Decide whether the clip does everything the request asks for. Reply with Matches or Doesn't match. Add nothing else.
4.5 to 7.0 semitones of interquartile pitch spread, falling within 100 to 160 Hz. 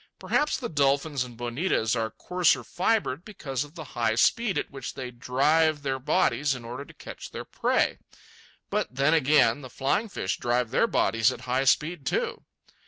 Doesn't match